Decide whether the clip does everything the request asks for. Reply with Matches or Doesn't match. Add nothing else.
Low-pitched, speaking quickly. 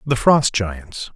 Doesn't match